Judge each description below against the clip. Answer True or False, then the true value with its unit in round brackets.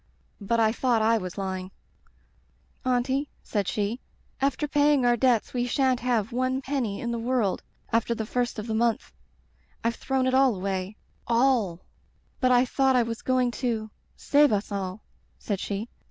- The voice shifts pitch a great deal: False (3.3 semitones)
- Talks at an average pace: True (185 wpm)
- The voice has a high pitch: True (235 Hz)